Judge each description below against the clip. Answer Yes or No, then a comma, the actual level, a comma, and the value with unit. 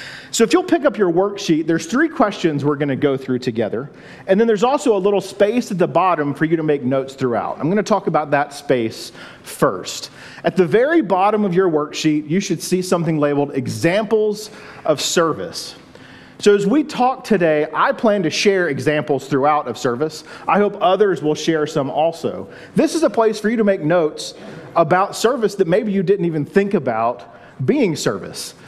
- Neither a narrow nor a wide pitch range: No, wide, 5.7 semitones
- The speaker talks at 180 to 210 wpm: Yes, average, 195 wpm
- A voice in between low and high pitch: Yes, medium, 180 Hz